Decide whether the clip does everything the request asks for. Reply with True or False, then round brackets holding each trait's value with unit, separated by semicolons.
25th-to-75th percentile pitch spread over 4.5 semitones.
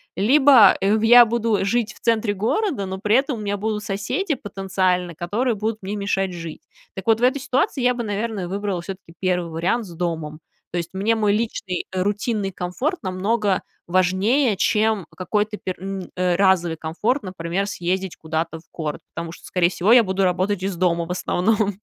False (3.6 semitones)